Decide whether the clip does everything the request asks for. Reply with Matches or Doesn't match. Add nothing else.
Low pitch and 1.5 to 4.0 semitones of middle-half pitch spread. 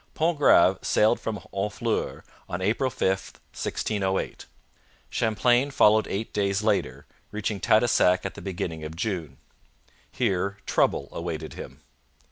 Matches